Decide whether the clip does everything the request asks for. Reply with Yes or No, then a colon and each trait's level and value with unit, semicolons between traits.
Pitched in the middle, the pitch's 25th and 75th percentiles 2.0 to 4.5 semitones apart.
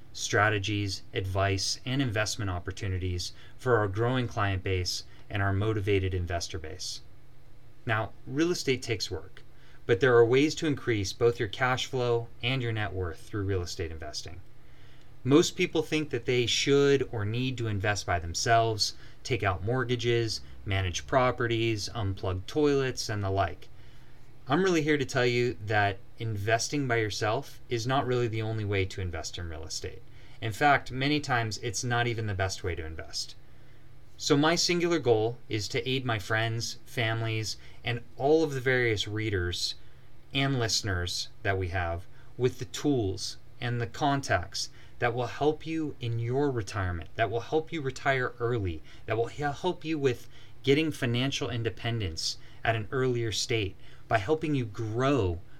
No: low, 115 Hz; average, 4.0 semitones